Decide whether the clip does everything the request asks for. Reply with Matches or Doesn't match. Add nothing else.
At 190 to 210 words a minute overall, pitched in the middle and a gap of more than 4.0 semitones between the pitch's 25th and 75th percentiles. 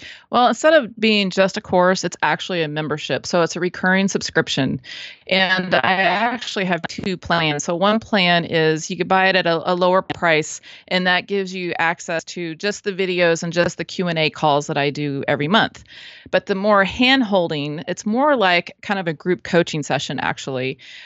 Doesn't match